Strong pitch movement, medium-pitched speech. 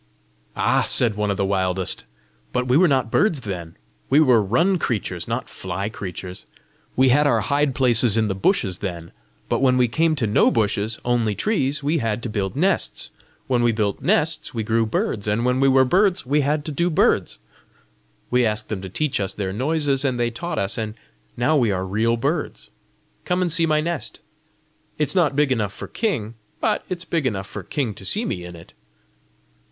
No: wide, 6.1 semitones; low, 120 Hz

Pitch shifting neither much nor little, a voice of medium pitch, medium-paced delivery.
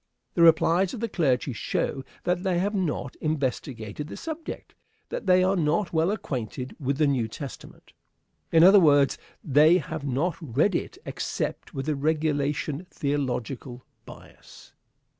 Yes: average, 4.5 semitones; medium, 150 Hz; average, 145 wpm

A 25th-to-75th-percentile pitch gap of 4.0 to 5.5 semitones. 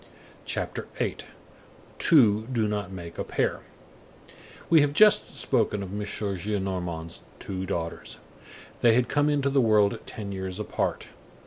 Yes: average, 4.4 semitones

